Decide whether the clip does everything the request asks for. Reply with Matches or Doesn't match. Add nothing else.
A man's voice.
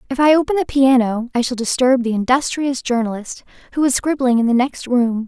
Doesn't match